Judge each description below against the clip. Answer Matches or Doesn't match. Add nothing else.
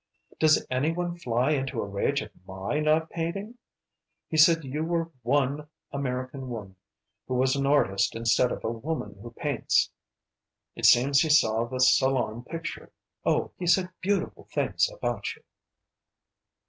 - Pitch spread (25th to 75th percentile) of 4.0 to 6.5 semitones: Matches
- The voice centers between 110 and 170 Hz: Matches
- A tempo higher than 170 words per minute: Doesn't match